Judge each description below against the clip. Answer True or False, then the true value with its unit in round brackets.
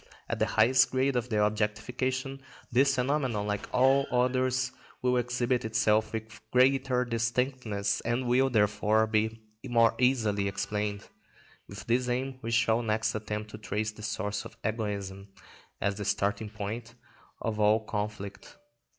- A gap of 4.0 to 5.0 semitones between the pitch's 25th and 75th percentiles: False (3.0 semitones)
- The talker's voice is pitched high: False (110 Hz)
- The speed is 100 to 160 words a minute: True (140 wpm)